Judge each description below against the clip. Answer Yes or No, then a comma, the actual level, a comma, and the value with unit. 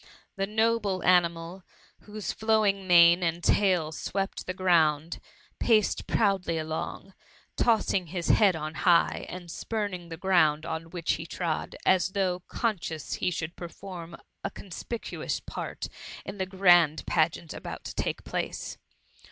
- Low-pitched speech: No, medium, 180 Hz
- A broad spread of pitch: No, average, 2.9 semitones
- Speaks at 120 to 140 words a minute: Yes, slow, 135 wpm